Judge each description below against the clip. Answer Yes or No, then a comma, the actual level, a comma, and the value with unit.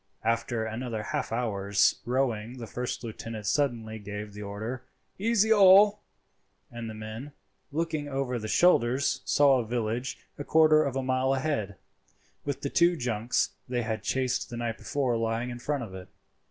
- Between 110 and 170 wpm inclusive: Yes, average, 165 wpm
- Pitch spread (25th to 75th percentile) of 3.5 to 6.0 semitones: Yes, average, 4.0 semitones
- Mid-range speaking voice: No, low, 120 Hz